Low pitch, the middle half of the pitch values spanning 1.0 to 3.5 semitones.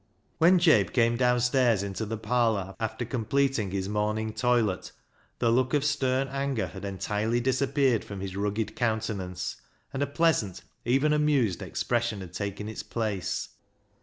No: low, 115 Hz; average, 4.3 semitones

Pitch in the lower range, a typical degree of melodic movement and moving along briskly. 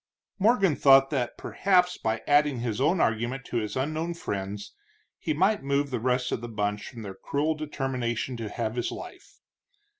No: low, 130 Hz; average, 4.9 semitones; average, 175 wpm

